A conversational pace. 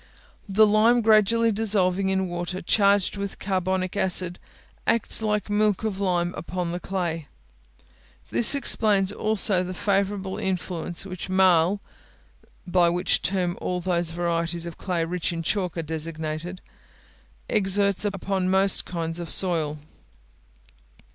No: slow, 130 wpm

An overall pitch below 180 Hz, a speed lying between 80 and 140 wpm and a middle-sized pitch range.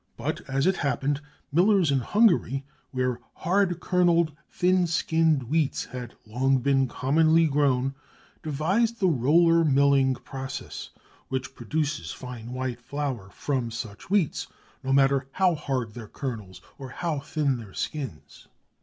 Yes: medium, 140 Hz; slow, 135 wpm; average, 4.2 semitones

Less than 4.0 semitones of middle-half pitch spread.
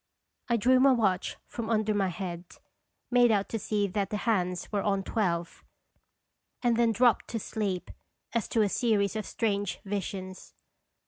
Yes: average, 3.0 semitones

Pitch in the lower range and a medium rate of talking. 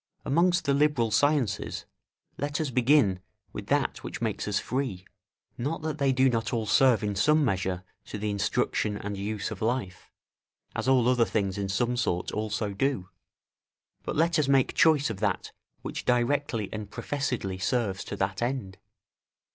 Yes: low, 120 Hz; average, 165 wpm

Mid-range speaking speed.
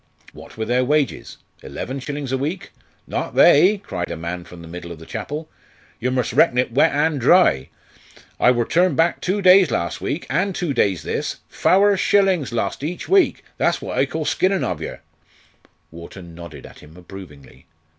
Yes: average, 185 wpm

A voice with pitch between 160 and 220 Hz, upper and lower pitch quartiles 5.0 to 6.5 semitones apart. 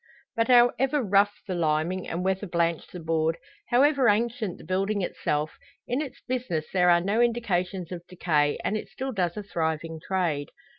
Yes: medium, 185 Hz; wide, 5.5 semitones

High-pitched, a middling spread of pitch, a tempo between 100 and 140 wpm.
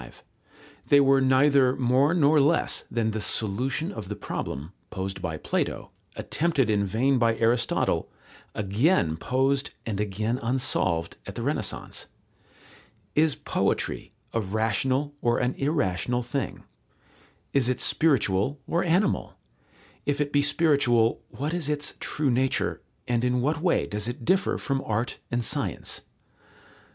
No: low, 125 Hz; average, 4.6 semitones; slow, 135 wpm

